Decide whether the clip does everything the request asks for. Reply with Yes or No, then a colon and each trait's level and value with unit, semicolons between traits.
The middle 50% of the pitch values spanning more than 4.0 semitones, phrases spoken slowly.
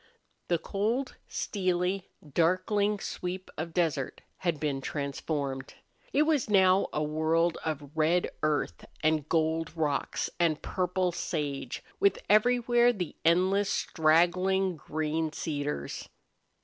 No: average, 3.7 semitones; slow, 110 wpm